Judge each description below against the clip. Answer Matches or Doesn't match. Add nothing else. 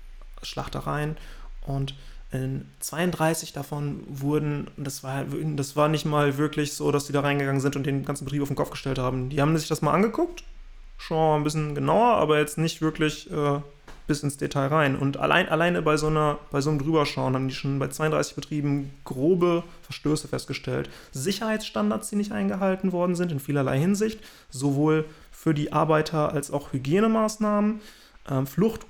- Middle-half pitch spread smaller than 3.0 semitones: Matches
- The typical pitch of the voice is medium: Matches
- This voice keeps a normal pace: Matches